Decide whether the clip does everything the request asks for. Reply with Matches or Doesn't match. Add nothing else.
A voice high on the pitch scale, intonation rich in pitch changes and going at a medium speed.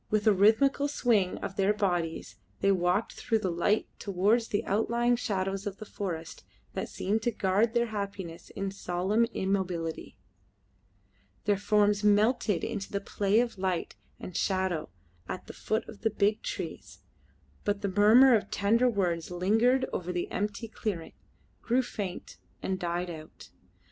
Doesn't match